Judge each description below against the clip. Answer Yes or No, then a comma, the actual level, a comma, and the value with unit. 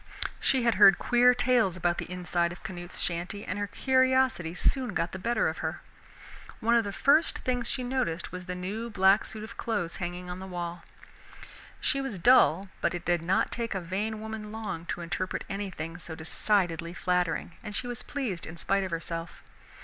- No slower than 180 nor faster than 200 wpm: Yes, average, 195 wpm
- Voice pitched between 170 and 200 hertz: Yes, high, 190 Hz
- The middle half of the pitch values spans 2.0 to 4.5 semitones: No, average, 4.9 semitones